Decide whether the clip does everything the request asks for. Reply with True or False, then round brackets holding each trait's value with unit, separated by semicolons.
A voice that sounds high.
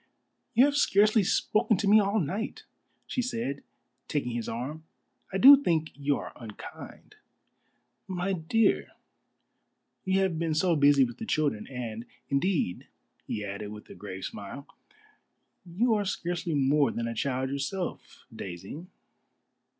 False (155 Hz)